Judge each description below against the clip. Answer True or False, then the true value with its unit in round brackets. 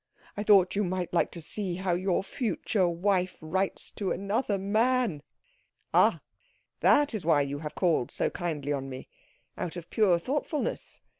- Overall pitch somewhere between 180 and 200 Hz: True (185 Hz)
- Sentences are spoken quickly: False (160 wpm)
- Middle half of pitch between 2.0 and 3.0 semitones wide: False (3.6 semitones)